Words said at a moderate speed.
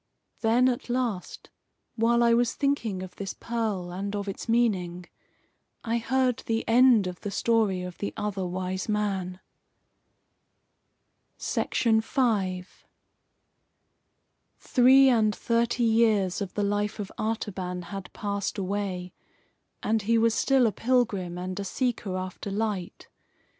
No: slow, 125 wpm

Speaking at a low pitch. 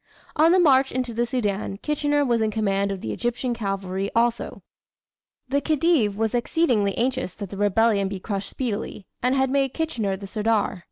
No: high, 230 Hz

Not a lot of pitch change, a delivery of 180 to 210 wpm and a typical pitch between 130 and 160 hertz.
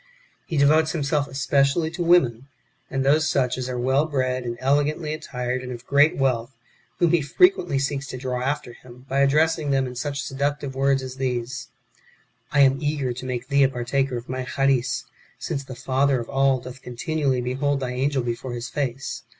Yes: narrow, 2.2 semitones; average, 190 wpm; low, 135 Hz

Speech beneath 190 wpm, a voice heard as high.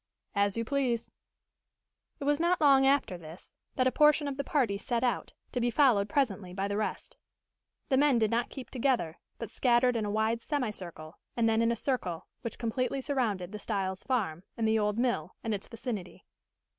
No: average, 195 wpm; high, 230 Hz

